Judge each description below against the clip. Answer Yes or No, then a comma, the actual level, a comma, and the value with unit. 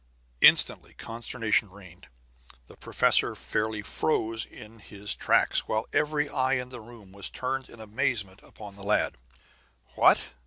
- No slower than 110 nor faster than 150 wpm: Yes, average, 140 wpm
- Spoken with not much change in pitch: No, average, 3.7 semitones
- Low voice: Yes, low, 110 Hz